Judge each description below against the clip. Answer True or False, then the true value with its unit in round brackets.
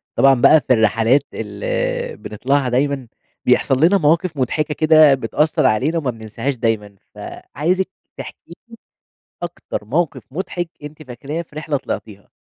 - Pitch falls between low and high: True (145 Hz)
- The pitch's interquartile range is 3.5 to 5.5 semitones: True (4.7 semitones)